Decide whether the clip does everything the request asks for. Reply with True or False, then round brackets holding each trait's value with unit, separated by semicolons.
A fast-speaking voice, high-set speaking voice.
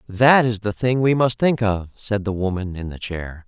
False (240 wpm; 105 Hz)